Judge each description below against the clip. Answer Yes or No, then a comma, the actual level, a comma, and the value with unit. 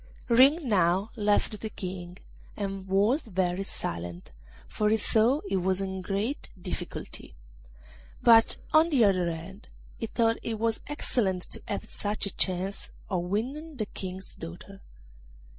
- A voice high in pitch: Yes, high, 200 Hz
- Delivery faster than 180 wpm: No, average, 145 wpm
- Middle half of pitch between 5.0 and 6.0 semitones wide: No, average, 3.5 semitones